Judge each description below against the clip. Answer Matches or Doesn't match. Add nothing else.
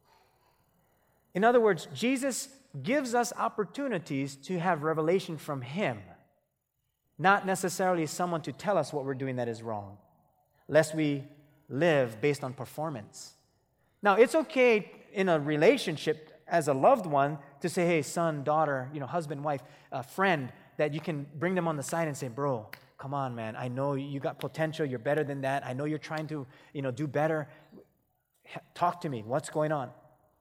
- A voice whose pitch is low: Doesn't match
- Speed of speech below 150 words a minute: Doesn't match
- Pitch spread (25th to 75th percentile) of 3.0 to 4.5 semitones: Matches